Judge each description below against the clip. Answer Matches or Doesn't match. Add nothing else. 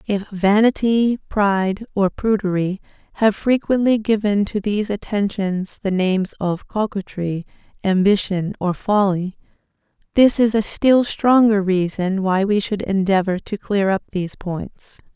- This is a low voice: Doesn't match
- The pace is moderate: Doesn't match